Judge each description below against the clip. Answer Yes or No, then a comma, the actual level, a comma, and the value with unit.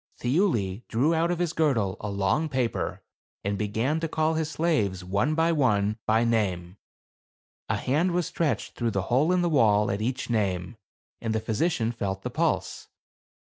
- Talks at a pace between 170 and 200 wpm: Yes, average, 175 wpm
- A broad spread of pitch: Yes, wide, 7.5 semitones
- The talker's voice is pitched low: Yes, low, 115 Hz